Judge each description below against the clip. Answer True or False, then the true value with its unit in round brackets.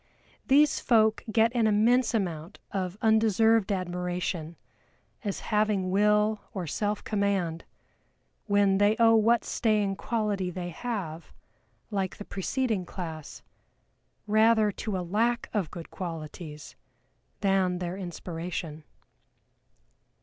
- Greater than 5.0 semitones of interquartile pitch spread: False (3.4 semitones)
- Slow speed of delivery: True (110 wpm)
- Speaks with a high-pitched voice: True (200 Hz)